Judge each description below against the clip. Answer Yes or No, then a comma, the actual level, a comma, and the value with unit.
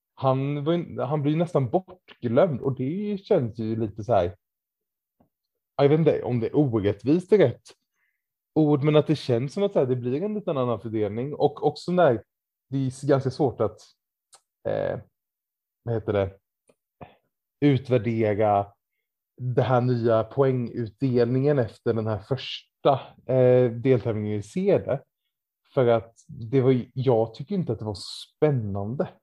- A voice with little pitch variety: No, average, 4.4 semitones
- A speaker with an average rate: Yes, average, 150 wpm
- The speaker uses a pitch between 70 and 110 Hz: No, low, 130 Hz